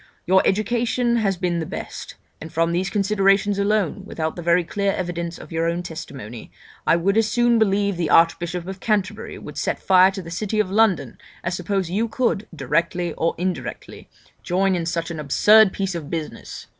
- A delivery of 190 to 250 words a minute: Yes, average, 195 wpm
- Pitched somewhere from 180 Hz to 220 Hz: Yes, medium, 185 Hz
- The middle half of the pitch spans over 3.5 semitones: No, average, 3.2 semitones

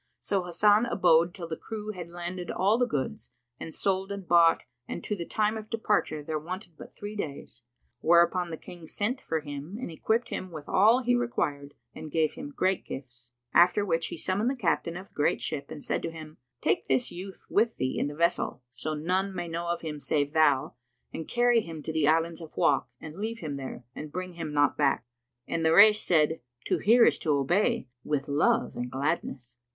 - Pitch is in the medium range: Yes, medium, 170 Hz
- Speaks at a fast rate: Yes, fast, 210 wpm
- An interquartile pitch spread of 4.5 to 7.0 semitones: Yes, average, 4.9 semitones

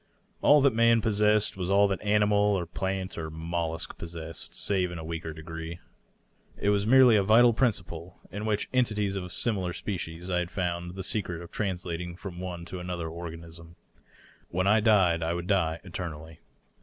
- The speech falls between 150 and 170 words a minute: No, average, 180 wpm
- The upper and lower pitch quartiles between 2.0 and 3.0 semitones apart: No, average, 3.4 semitones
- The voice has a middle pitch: No, very low, 90 Hz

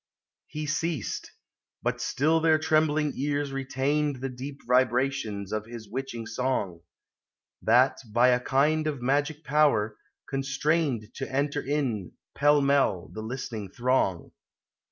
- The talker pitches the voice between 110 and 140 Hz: Yes, low, 135 Hz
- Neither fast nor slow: No, slow, 125 wpm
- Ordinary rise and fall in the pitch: Yes, average, 3.7 semitones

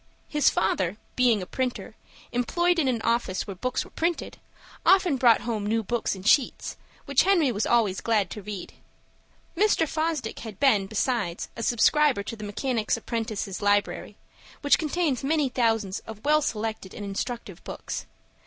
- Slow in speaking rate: No, average, 160 wpm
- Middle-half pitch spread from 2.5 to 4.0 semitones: No, average, 5.3 semitones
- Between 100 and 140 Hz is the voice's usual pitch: No, high, 230 Hz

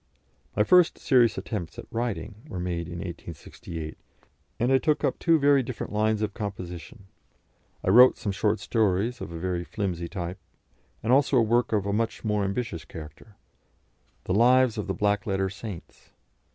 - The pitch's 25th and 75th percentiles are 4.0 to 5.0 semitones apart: Yes, average, 4.6 semitones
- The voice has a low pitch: Yes, low, 105 Hz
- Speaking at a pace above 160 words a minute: Yes, average, 170 wpm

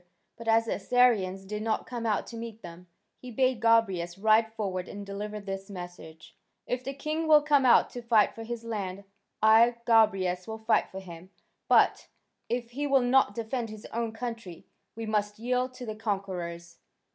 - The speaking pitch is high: Yes, high, 220 Hz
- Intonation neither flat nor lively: Yes, average, 3.6 semitones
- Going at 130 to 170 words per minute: No, average, 180 wpm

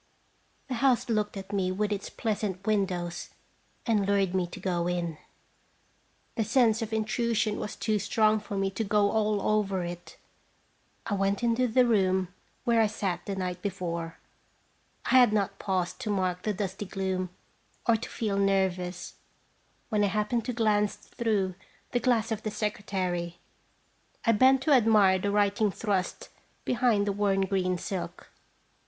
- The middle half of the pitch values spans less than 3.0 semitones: Yes, narrow, 2.6 semitones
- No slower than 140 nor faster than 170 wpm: Yes, average, 160 wpm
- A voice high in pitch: Yes, high, 205 Hz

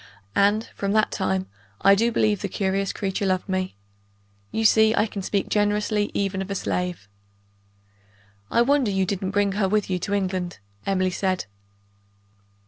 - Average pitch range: No, narrow, 1.9 semitones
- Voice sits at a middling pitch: No, high, 195 Hz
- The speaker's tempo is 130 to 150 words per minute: No, average, 160 wpm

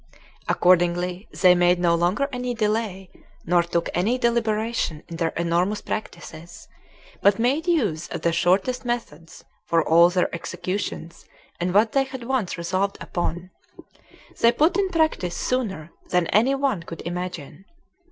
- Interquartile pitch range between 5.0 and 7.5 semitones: Yes, wide, 5.5 semitones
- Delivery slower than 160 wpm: Yes, average, 140 wpm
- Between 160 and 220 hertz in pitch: Yes, medium, 185 Hz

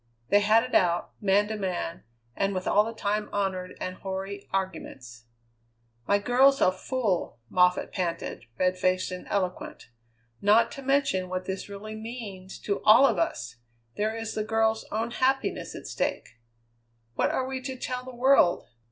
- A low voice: No, high, 205 Hz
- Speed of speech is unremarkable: Yes, average, 165 wpm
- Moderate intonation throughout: Yes, average, 3.7 semitones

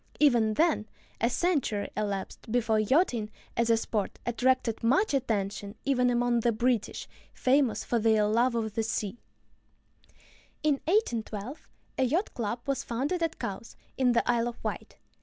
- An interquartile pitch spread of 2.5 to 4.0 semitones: Yes, average, 3.2 semitones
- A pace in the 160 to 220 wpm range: No, average, 150 wpm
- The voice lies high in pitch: Yes, high, 235 Hz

